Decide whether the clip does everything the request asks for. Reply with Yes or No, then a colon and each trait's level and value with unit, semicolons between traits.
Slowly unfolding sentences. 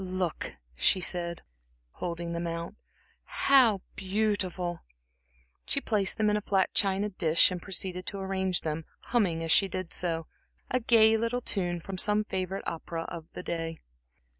No: average, 155 wpm